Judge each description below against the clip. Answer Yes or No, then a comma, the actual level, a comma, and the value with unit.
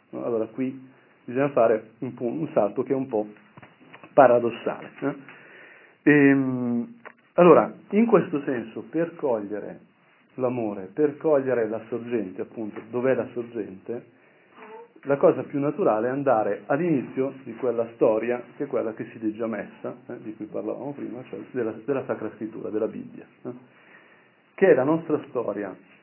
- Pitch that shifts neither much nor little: Yes, average, 3.3 semitones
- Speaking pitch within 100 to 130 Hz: Yes, low, 125 Hz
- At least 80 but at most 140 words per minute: No, average, 150 wpm